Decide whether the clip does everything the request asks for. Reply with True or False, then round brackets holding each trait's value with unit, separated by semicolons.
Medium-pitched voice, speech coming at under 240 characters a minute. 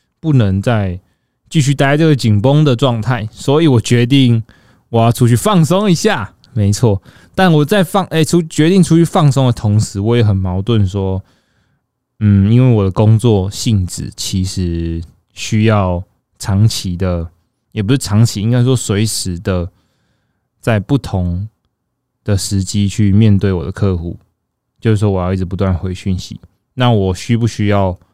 False (110 Hz; 230 characters per minute)